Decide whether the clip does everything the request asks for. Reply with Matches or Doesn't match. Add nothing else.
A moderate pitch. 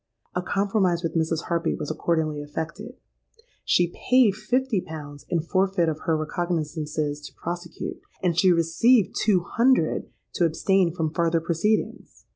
Matches